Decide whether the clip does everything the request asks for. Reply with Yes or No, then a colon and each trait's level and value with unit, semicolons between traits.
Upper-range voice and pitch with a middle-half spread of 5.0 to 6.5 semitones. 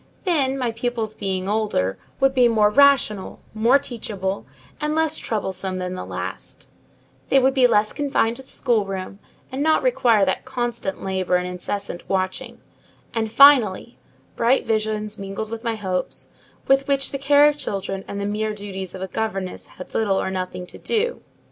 Yes: high, 220 Hz; wide, 5.4 semitones